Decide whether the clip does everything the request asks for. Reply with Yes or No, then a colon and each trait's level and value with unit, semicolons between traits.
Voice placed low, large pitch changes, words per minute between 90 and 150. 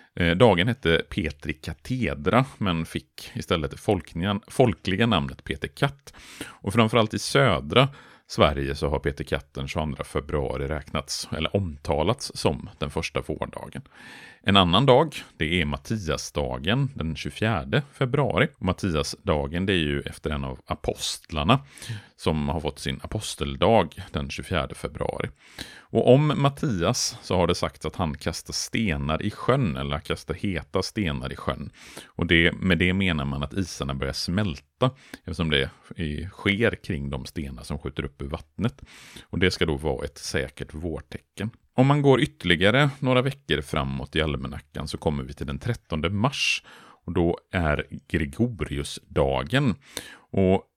Yes: very low, 85 Hz; wide, 6.6 semitones; average, 145 wpm